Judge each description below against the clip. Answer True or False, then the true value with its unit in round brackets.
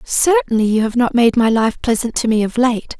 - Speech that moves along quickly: True (240 wpm)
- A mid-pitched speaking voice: False (230 Hz)